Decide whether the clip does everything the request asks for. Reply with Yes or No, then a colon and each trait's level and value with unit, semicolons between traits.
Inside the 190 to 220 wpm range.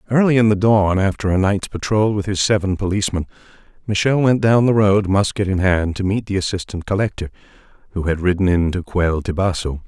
Yes: average, 195 wpm